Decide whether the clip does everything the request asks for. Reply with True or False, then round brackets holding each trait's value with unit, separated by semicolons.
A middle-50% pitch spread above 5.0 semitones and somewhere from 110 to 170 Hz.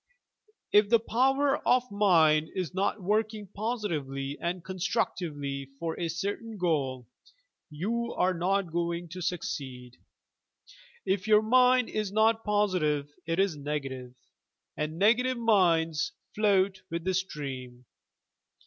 False (5.6 semitones; 185 Hz)